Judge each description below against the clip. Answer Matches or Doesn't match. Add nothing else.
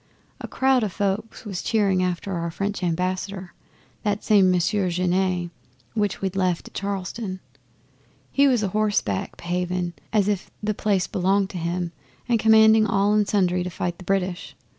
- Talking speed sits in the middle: Matches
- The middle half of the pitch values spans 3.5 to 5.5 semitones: Doesn't match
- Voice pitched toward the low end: Doesn't match